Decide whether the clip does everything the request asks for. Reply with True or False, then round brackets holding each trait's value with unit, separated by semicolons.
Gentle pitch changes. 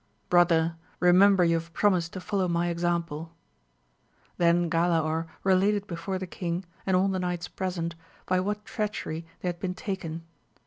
True (2.0 semitones)